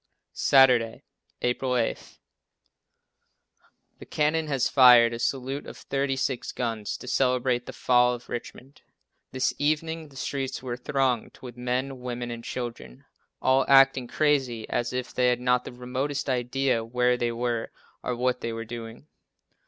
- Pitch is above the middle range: No, low, 125 Hz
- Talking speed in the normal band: Yes, average, 150 wpm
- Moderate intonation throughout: No, narrow, 1.9 semitones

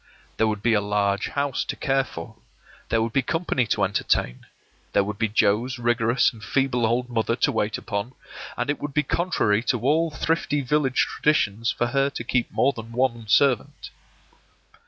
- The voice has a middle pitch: No, low, 120 Hz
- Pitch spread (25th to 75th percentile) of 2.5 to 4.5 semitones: Yes, average, 3.9 semitones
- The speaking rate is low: No, average, 180 wpm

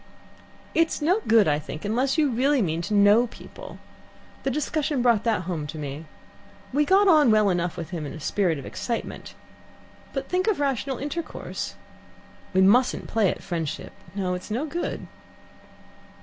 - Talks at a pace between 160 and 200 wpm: Yes, average, 165 wpm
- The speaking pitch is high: Yes, high, 220 Hz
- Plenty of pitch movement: Yes, wide, 8.3 semitones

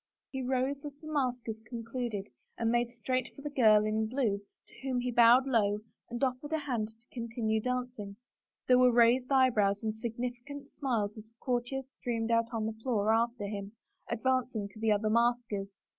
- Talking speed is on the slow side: No, average, 185 wpm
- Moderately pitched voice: No, high, 235 Hz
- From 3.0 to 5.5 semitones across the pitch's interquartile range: No, narrow, 2.6 semitones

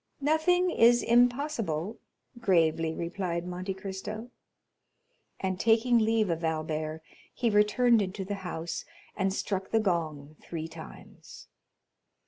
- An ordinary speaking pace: No, slow, 110 wpm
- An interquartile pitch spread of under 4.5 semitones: No, wide, 5.6 semitones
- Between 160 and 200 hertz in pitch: Yes, high, 190 Hz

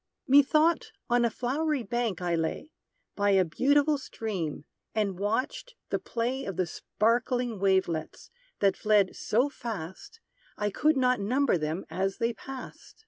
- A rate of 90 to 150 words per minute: Yes, average, 140 wpm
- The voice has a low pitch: No, high, 230 Hz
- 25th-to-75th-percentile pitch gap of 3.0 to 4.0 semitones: No, wide, 5.5 semitones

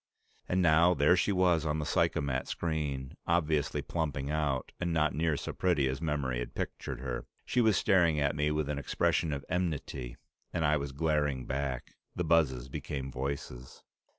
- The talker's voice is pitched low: Yes, very low, 75 Hz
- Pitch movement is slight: No, average, 3.4 semitones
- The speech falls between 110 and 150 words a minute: No, average, 175 wpm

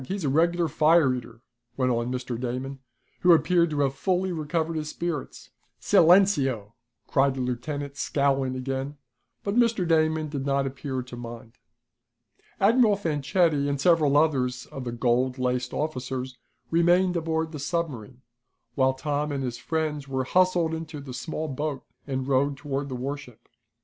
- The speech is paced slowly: No, average, 155 wpm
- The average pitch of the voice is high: No, medium, 140 Hz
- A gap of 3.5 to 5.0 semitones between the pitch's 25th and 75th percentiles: Yes, average, 3.9 semitones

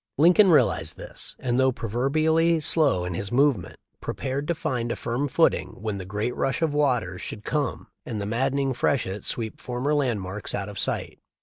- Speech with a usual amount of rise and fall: No, wide, 5.7 semitones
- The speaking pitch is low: Yes, low, 125 Hz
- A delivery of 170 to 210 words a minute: Yes, average, 185 wpm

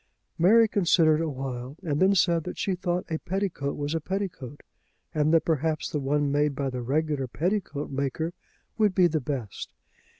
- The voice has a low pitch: No, medium, 155 Hz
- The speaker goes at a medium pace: Yes, average, 175 wpm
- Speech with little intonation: No, average, 4.0 semitones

